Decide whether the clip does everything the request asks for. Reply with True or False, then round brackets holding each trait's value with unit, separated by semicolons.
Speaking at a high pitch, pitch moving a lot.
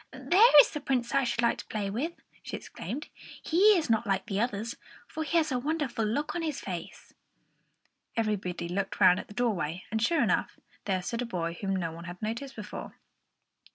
True (230 Hz; 6.6 semitones)